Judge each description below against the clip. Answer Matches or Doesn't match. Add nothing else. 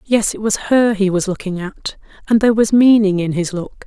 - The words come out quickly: Matches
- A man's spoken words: Doesn't match